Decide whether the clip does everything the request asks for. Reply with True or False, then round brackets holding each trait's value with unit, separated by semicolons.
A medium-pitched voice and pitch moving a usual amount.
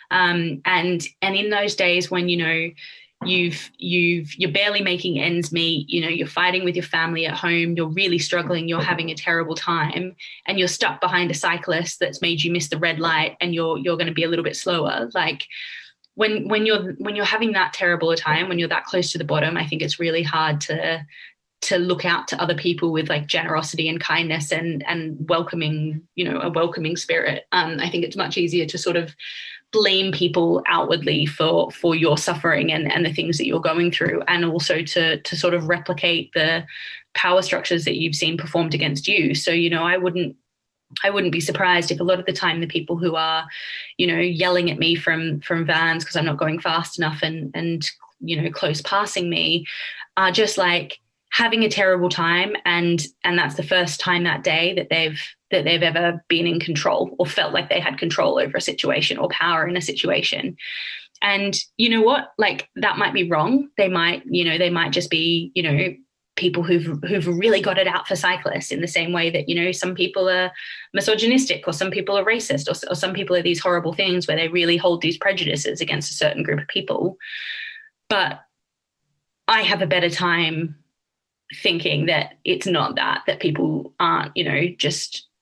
False (170 Hz; 1.9 semitones)